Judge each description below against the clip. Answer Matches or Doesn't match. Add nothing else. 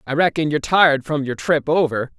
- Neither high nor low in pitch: Matches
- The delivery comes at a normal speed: Doesn't match